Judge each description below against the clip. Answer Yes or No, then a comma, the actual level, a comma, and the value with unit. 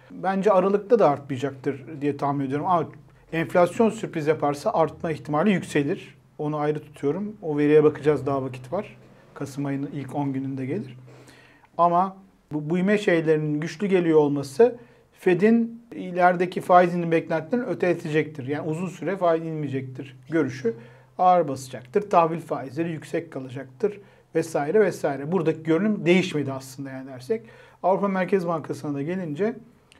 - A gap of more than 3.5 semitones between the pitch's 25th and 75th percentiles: Yes, average, 4.2 semitones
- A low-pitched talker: No, medium, 160 Hz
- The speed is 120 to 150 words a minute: Yes, average, 135 wpm